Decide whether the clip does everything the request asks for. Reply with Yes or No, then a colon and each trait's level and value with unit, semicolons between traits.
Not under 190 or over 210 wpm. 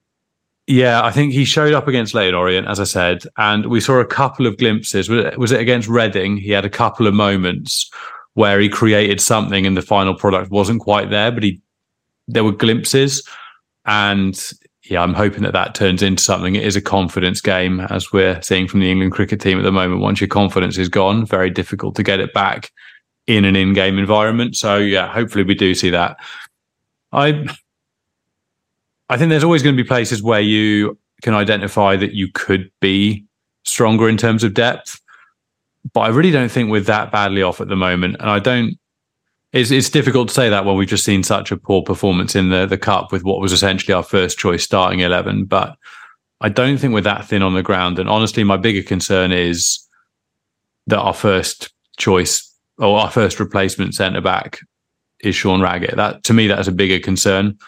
Yes: average, 200 wpm